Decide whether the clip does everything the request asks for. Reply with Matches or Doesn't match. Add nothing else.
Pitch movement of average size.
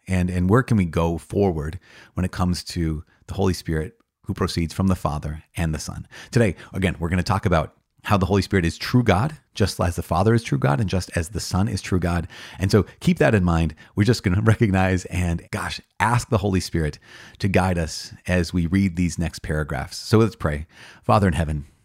Matches